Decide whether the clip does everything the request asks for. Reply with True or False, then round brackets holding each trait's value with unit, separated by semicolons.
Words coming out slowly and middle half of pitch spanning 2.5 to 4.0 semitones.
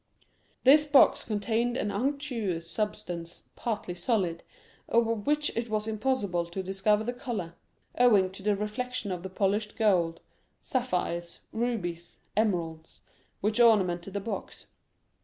False (125 wpm; 4.6 semitones)